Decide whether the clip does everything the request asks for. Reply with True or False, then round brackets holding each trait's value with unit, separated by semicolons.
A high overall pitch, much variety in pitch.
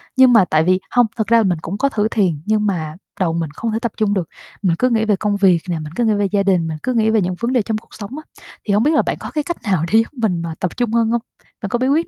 False (210 Hz; 4.3 semitones)